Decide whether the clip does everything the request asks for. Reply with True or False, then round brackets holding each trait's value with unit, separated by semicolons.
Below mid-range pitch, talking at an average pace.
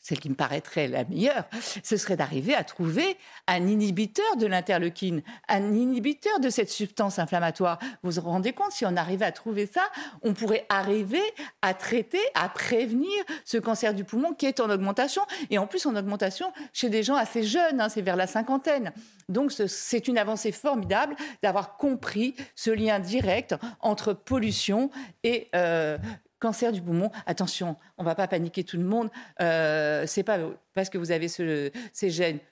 False (215 Hz; 180 wpm)